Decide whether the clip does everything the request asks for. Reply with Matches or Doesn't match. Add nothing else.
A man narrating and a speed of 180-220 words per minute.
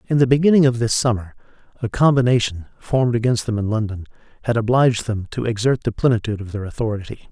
Matches